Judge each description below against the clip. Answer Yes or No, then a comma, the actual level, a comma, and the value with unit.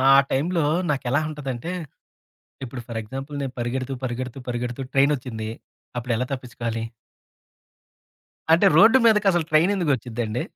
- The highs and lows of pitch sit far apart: No, average, 3.9 semitones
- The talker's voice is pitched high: No, low, 130 Hz